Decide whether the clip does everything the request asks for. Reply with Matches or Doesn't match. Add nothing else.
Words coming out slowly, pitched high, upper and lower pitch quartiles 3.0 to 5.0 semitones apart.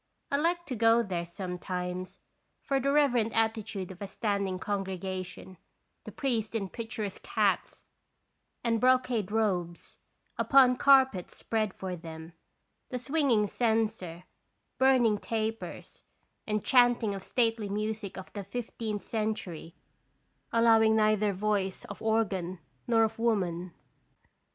Matches